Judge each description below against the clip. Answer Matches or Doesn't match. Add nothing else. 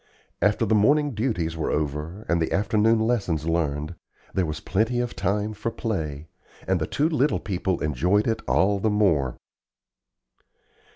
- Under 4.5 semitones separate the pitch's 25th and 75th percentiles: Doesn't match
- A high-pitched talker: Doesn't match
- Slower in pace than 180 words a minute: Matches